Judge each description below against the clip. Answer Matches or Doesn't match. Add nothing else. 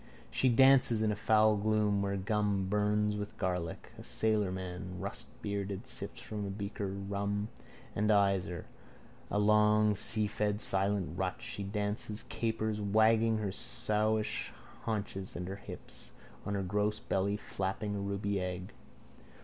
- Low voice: Matches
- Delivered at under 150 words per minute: Matches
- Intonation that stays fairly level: Matches